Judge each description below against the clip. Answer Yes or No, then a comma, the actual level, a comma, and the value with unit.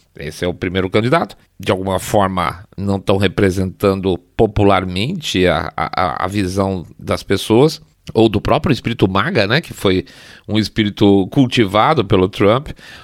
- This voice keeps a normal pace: Yes, average, 145 wpm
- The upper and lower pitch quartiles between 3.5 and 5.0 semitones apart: No, average, 2.9 semitones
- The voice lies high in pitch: No, low, 100 Hz